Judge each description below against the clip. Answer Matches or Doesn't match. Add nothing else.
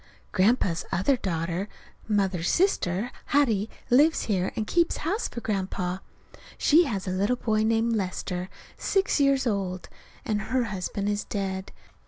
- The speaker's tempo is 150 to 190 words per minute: Doesn't match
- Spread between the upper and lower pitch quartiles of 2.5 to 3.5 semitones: Doesn't match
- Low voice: Doesn't match